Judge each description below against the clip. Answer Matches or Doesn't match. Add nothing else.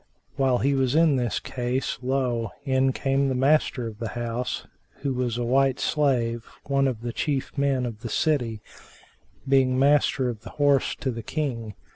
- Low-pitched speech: Matches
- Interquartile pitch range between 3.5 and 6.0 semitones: Doesn't match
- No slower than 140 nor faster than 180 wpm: Matches